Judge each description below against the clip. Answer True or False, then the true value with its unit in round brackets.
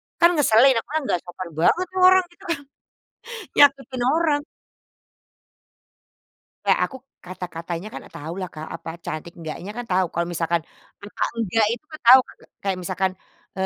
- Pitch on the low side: False (200 Hz)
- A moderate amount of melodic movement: False (8.3 semitones)